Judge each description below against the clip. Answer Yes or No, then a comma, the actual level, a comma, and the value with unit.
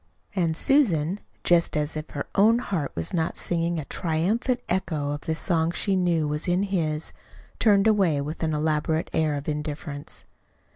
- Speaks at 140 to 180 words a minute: Yes, average, 165 wpm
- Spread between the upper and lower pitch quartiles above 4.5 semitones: No, average, 3.7 semitones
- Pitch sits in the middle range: Yes, medium, 160 Hz